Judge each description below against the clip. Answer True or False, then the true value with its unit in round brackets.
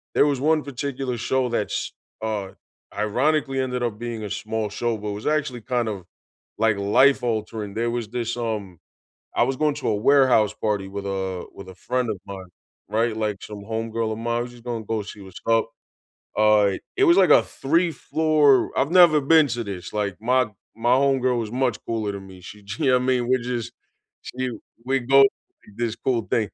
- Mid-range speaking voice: False (120 Hz)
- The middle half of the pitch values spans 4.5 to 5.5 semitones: False (3.7 semitones)